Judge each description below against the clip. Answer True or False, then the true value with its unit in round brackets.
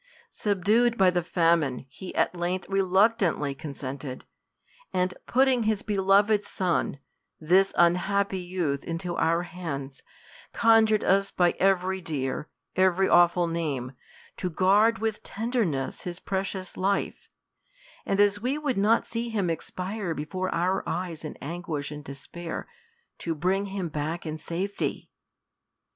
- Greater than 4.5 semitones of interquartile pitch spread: False (3.3 semitones)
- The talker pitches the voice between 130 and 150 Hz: False (185 Hz)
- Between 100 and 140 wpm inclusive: True (135 wpm)